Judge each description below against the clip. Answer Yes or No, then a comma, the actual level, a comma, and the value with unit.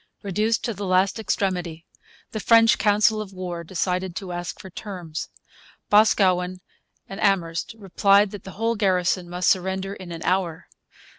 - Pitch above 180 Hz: Yes, high, 190 Hz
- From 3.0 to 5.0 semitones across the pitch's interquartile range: No, narrow, 2.4 semitones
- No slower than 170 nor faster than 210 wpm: No, average, 150 wpm